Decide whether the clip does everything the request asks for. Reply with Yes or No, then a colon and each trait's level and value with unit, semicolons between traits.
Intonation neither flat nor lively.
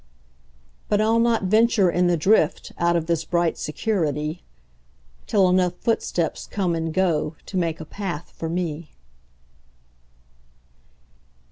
Yes: average, 3.6 semitones